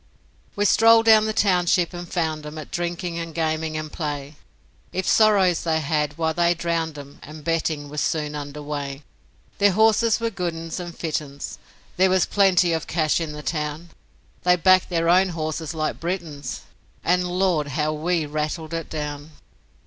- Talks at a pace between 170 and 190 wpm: Yes, average, 175 wpm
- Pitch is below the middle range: No, medium, 165 Hz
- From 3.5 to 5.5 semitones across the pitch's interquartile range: No, average, 2.8 semitones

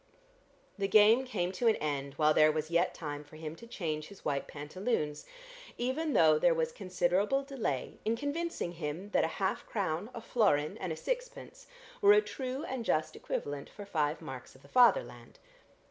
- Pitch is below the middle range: No, medium, 180 Hz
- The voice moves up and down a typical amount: No, wide, 7.8 semitones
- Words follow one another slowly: No, average, 180 wpm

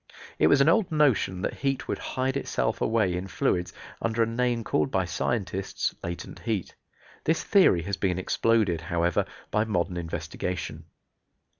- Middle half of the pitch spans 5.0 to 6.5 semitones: Yes, wide, 5.5 semitones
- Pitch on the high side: No, low, 100 Hz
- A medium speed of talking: Yes, average, 155 wpm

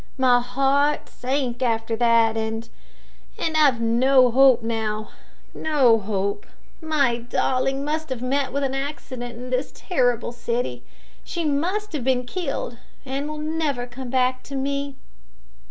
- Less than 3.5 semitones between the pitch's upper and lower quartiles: Yes, average, 3.1 semitones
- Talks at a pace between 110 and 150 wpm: Yes, average, 140 wpm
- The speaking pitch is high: Yes, very high, 255 Hz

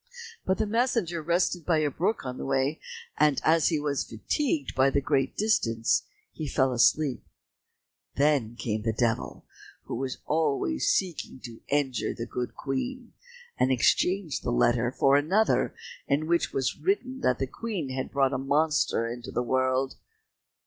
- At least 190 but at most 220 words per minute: No, average, 160 wpm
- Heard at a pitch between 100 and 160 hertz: Yes, medium, 140 Hz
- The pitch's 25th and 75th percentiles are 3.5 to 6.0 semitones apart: Yes, average, 4.6 semitones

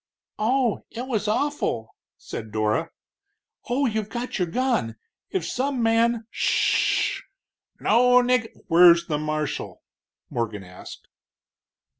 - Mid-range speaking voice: No, high, 220 Hz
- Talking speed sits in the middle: No, slow, 130 wpm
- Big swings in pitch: Yes, wide, 8.3 semitones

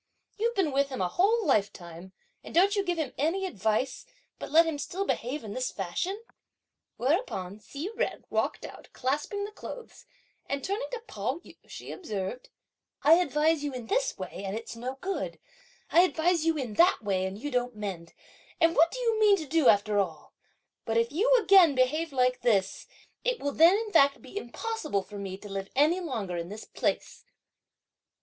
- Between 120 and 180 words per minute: No, average, 190 wpm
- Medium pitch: No, very high, 280 Hz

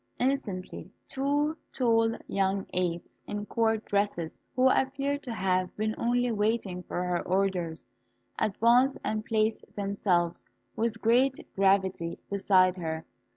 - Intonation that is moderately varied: Yes, average, 4.2 semitones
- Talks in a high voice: Yes, high, 210 Hz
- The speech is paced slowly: Yes, slow, 120 wpm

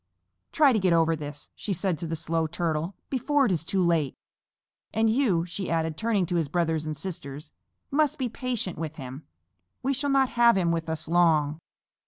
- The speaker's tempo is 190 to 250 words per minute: Yes, average, 200 wpm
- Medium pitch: Yes, medium, 170 Hz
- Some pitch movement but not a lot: No, wide, 5.7 semitones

